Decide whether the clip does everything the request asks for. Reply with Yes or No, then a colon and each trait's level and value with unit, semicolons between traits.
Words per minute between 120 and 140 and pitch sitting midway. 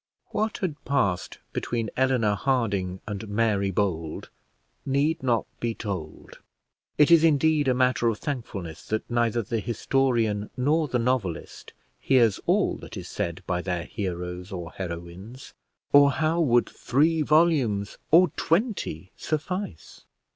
No: slow, 135 wpm; low, 120 Hz